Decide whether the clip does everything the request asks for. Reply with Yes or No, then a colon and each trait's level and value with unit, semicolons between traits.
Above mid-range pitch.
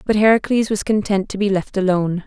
Yes: high, 200 Hz